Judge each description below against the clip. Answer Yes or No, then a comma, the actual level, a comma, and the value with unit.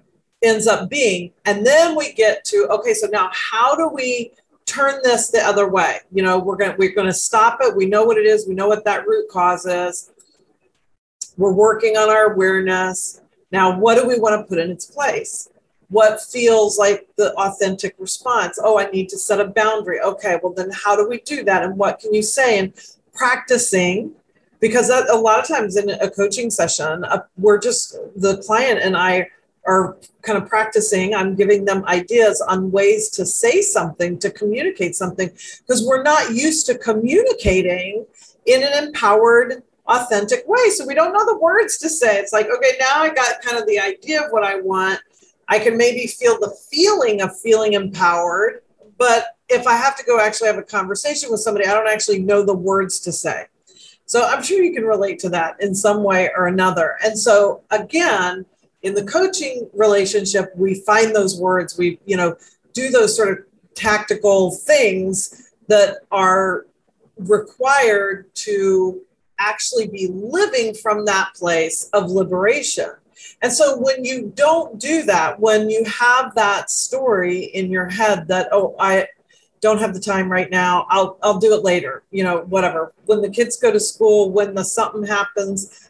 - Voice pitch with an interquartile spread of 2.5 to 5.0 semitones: Yes, average, 4.4 semitones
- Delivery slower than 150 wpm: No, average, 185 wpm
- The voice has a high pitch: Yes, high, 210 Hz